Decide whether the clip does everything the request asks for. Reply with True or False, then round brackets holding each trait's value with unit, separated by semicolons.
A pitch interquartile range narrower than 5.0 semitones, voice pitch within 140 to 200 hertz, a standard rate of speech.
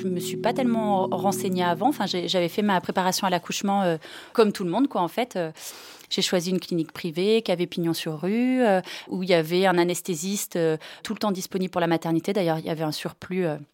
False (2.6 semitones; 185 Hz; 245 wpm)